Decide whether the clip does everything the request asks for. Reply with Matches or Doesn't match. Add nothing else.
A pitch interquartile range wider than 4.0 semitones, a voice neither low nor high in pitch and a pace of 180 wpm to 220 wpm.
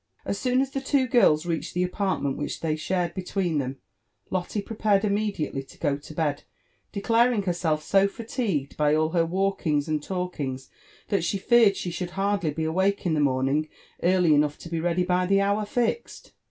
Matches